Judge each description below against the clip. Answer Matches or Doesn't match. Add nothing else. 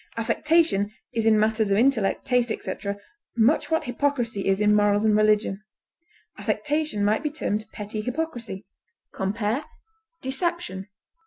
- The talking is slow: Matches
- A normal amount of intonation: Matches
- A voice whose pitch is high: Matches